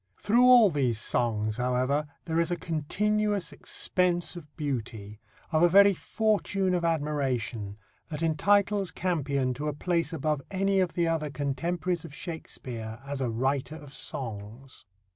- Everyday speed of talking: Yes, average, 145 wpm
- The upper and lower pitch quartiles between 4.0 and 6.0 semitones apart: Yes, wide, 5.5 semitones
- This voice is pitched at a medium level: Yes, medium, 150 Hz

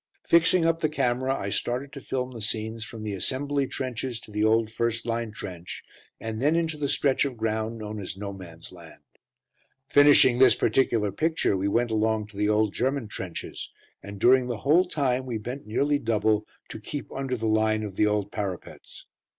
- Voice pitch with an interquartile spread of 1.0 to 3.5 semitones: No, average, 3.9 semitones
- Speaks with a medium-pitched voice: No, low, 115 Hz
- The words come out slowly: No, average, 190 wpm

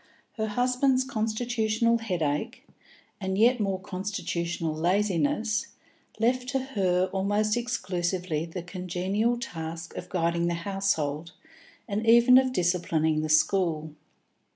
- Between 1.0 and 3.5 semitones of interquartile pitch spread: No, average, 4.9 semitones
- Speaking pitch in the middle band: No, high, 195 Hz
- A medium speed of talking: No, slow, 110 wpm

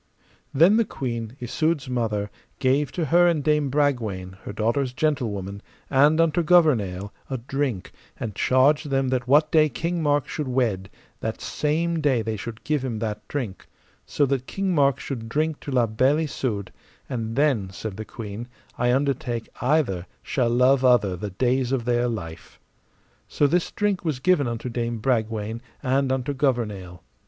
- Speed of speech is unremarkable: Yes, average, 165 wpm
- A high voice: No, low, 130 Hz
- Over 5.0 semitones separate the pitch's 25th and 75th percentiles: No, average, 4.5 semitones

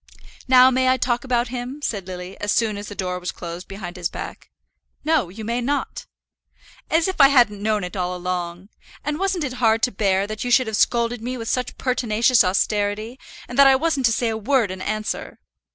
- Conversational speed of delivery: No, fast, 215 wpm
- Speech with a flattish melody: No, average, 4.5 semitones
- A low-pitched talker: No, high, 225 Hz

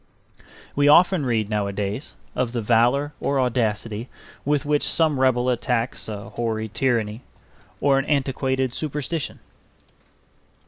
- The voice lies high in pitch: No, low, 125 Hz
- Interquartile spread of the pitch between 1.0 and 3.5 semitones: No, average, 3.9 semitones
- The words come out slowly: Yes, slow, 120 wpm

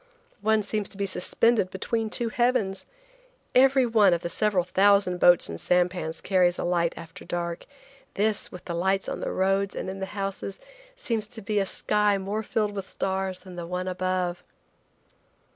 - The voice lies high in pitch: Yes, high, 195 Hz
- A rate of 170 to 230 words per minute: Yes, average, 175 wpm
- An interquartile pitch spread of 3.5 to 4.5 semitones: No, average, 2.7 semitones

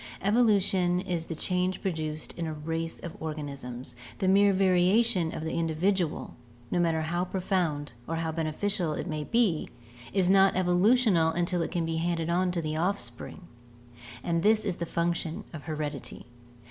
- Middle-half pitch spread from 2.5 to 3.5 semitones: Yes, average, 2.8 semitones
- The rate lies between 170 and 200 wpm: No, average, 160 wpm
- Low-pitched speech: No, medium, 170 Hz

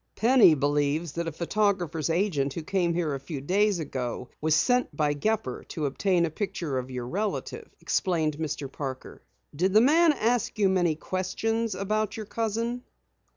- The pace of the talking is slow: No, average, 165 wpm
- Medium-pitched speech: Yes, medium, 175 Hz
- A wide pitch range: Yes, wide, 6.3 semitones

